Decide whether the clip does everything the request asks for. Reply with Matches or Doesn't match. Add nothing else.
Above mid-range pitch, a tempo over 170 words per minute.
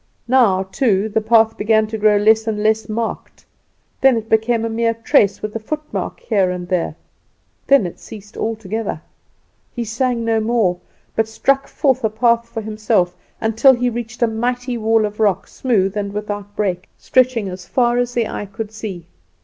Matches